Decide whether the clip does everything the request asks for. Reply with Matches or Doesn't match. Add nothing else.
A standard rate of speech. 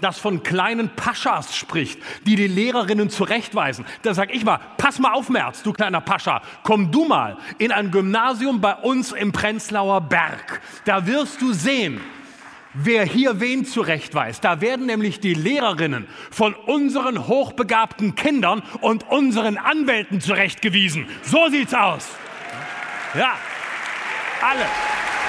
Matches